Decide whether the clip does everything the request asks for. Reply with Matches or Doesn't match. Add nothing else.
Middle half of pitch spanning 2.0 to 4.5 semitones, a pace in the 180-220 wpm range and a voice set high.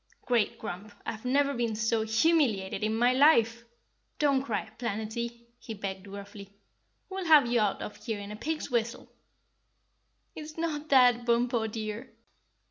Doesn't match